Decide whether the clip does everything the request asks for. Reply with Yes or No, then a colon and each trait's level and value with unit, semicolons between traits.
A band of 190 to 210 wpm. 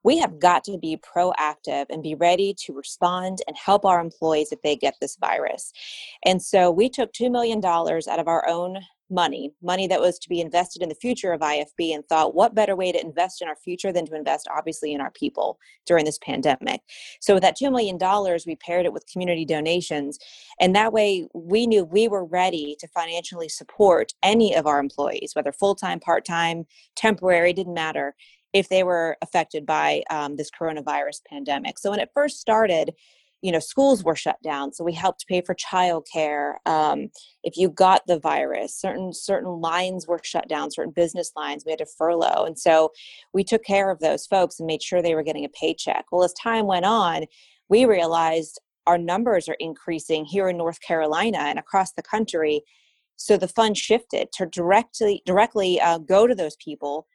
Yes: average, 195 wpm